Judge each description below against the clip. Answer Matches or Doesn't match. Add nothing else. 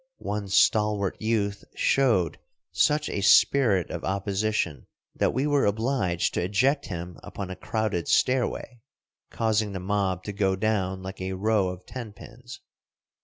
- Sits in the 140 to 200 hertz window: Doesn't match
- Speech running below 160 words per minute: Matches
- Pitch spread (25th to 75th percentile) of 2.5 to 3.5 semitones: Matches